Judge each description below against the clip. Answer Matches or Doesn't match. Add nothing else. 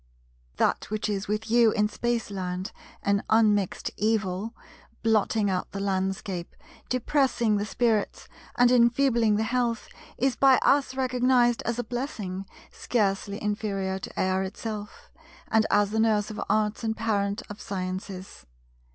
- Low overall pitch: Doesn't match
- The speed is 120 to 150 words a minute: Matches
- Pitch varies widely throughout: Doesn't match